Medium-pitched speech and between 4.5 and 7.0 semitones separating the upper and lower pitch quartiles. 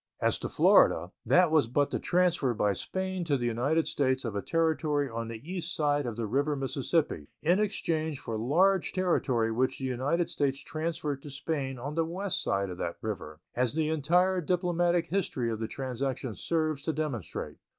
Yes: medium, 145 Hz; average, 5.3 semitones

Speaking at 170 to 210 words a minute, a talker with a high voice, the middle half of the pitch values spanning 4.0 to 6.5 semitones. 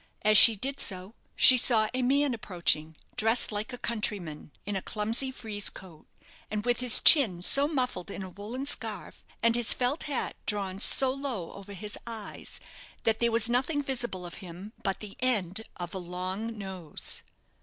Yes: average, 175 wpm; high, 215 Hz; average, 4.5 semitones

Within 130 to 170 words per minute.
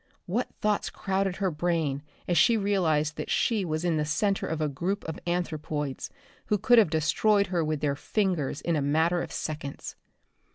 No: average, 180 wpm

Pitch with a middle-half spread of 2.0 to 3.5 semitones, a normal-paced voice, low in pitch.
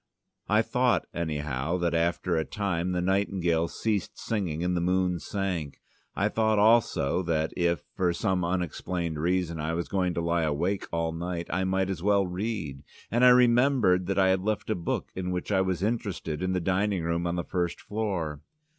Yes: average, 2.8 semitones; average, 190 wpm; very low, 90 Hz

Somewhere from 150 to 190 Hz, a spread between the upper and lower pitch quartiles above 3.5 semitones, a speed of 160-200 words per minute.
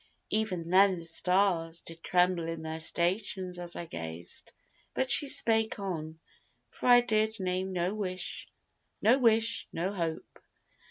No: medium, 185 Hz; average, 4.4 semitones; average, 145 wpm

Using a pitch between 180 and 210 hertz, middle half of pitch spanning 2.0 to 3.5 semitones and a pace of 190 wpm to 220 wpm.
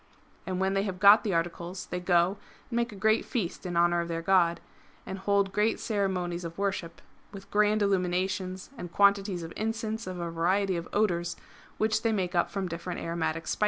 Yes: high, 190 Hz; average, 2.8 semitones; average, 195 wpm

